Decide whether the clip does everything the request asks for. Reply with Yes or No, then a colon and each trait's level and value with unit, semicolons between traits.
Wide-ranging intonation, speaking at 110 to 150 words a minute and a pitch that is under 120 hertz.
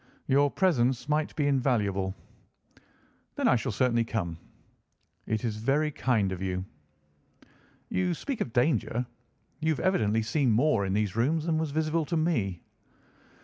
No: wide, 6.4 semitones; average, 145 wpm; low, 125 Hz